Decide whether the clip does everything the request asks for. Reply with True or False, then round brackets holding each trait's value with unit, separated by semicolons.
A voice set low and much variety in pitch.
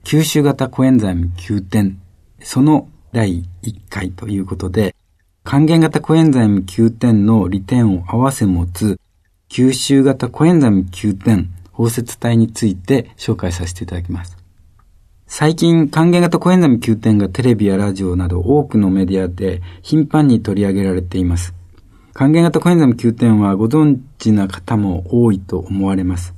True (105 Hz; 5.8 semitones)